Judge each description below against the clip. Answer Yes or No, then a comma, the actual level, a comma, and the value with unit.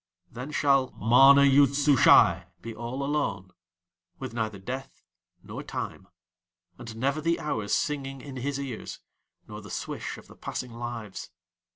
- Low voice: Yes, low, 130 Hz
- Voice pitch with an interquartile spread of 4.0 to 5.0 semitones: No, average, 3.5 semitones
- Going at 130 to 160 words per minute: Yes, average, 145 wpm